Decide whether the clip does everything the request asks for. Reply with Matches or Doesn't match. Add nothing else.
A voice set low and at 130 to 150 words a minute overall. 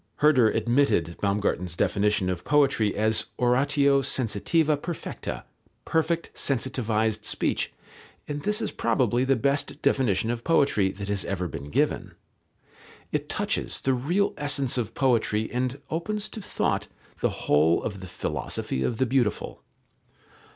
Matches